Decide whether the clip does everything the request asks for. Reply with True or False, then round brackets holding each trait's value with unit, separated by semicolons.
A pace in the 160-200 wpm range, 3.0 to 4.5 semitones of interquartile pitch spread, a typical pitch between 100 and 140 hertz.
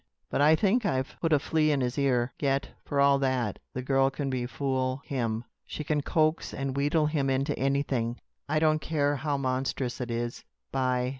False (190 wpm; 2.4 semitones; 135 Hz)